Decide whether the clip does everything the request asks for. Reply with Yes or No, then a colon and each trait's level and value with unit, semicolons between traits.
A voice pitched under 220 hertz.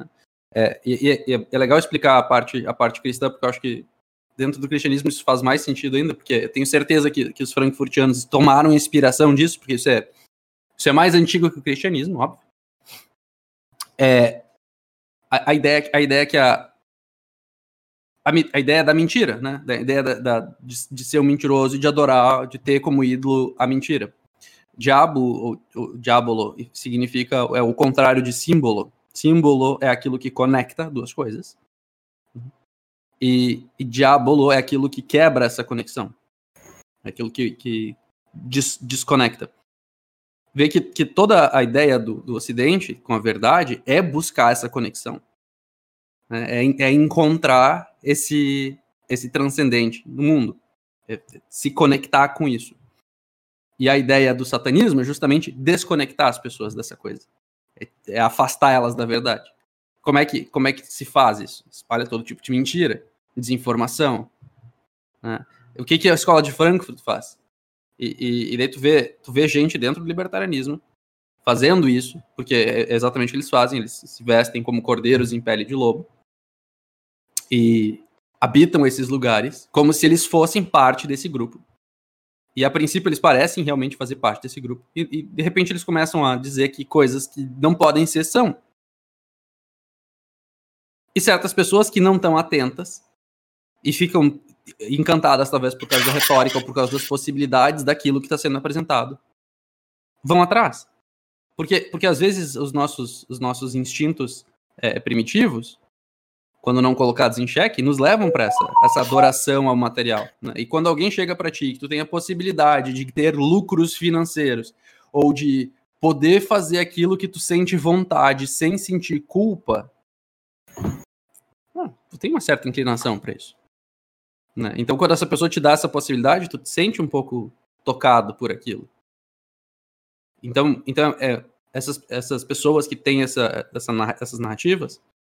Yes: low, 135 Hz